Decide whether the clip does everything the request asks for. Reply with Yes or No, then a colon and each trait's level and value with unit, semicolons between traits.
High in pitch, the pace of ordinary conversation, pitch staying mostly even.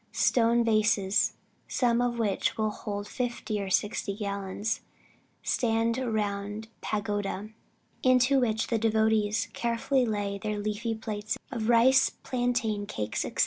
No: high, 220 Hz; slow, 130 wpm; narrow, 2.3 semitones